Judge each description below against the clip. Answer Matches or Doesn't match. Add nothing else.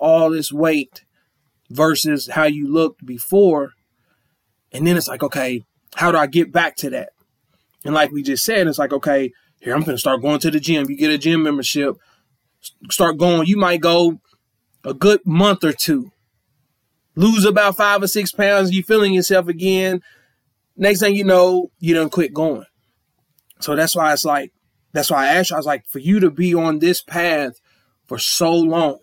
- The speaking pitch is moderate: Matches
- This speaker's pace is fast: Doesn't match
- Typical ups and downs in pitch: Matches